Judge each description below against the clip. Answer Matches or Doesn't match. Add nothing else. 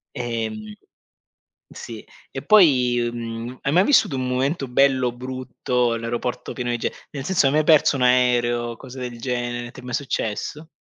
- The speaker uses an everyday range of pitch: Doesn't match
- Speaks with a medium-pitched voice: Doesn't match